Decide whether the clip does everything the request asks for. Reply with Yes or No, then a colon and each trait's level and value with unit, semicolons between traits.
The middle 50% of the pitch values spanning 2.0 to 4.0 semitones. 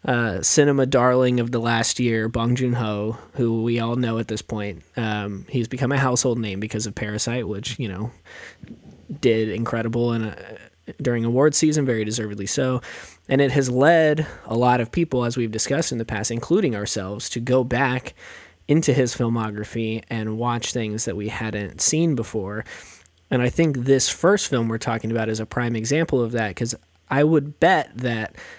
Yes: narrow, 2.6 semitones